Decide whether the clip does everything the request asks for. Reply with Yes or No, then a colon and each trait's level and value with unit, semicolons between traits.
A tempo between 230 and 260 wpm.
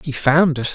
Yes: fast, 240 wpm